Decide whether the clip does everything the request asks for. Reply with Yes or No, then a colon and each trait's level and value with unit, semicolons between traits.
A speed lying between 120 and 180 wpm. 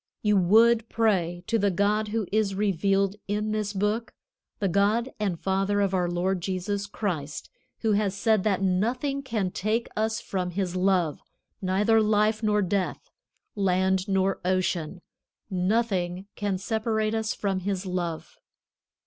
Yes: average, 145 wpm